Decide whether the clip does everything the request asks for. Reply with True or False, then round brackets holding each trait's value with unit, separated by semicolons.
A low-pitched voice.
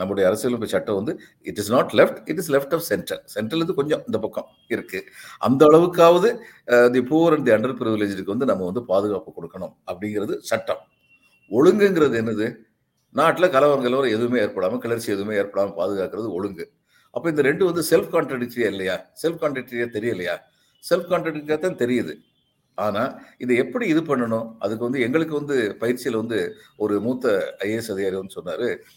True (130 Hz)